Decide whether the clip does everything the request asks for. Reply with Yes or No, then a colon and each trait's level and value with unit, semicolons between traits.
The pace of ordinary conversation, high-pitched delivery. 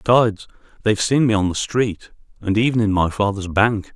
No: average, 195 wpm; low, 105 Hz